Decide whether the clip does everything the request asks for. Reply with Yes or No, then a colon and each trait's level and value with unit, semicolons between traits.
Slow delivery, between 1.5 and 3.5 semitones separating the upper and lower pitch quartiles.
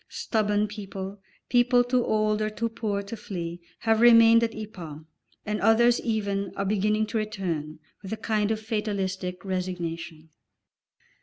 No: average, 145 wpm; narrow, 2.6 semitones